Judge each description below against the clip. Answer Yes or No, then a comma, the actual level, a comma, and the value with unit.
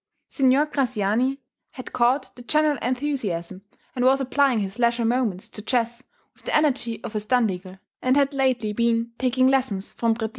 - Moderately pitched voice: No, high, 245 Hz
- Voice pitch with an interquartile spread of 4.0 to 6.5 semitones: No, average, 3.1 semitones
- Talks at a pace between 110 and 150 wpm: No, average, 170 wpm